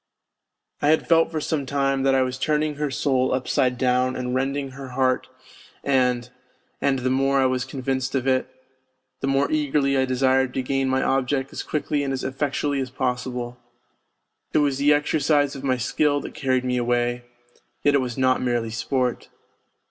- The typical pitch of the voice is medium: No, low, 130 Hz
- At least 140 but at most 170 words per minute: No, average, 180 wpm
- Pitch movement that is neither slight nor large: No, narrow, 1.6 semitones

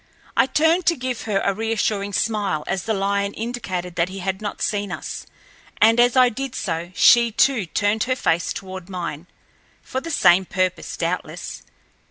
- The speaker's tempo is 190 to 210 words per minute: No, average, 175 wpm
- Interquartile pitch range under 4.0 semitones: No, average, 4.4 semitones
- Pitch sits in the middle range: No, high, 205 Hz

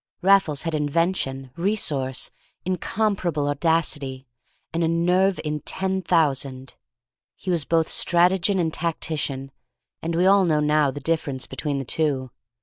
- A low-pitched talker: No, medium, 160 Hz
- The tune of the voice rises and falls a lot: No, average, 3.9 semitones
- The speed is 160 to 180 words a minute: No, slow, 135 wpm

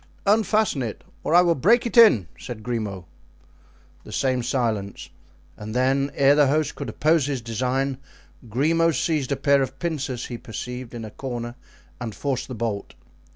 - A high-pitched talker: No, low, 130 Hz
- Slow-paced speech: No, average, 165 wpm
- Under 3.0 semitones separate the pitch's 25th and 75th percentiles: No, average, 4.2 semitones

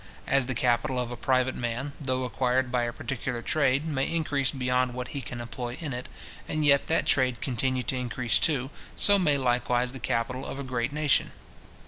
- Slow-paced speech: No, average, 195 wpm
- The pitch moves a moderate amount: No, narrow, 2.0 semitones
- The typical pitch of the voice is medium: No, low, 130 Hz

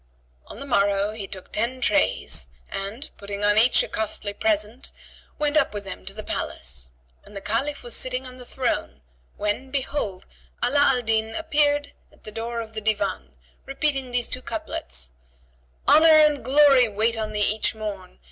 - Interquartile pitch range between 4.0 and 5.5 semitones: Yes, average, 4.6 semitones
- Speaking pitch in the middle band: No, high, 225 Hz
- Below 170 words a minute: No, average, 175 wpm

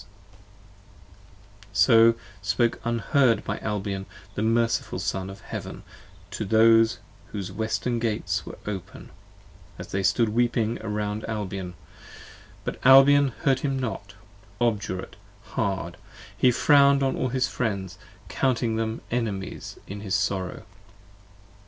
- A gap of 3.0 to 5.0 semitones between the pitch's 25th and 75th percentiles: Yes, average, 3.3 semitones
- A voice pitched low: Yes, low, 110 Hz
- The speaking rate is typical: No, slow, 120 wpm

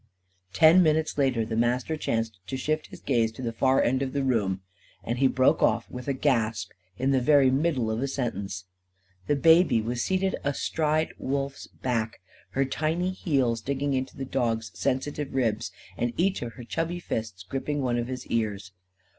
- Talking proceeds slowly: No, average, 180 wpm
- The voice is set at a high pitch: No, low, 130 Hz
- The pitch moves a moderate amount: Yes, average, 3.9 semitones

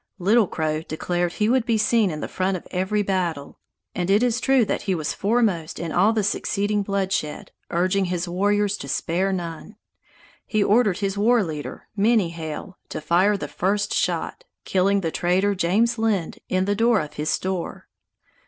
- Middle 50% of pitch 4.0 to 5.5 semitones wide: No, average, 3.3 semitones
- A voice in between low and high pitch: No, high, 195 Hz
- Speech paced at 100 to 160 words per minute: No, average, 180 wpm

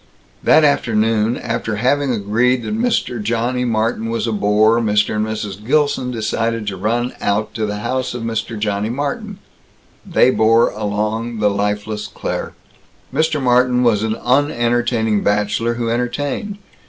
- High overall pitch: No, low, 115 Hz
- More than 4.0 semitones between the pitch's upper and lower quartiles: No, average, 2.8 semitones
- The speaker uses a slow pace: No, average, 145 wpm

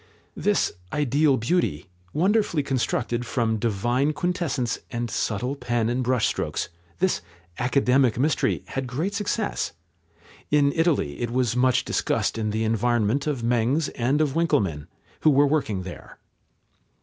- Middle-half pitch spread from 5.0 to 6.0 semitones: No, average, 4.2 semitones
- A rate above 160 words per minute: No, slow, 135 wpm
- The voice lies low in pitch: Yes, low, 130 Hz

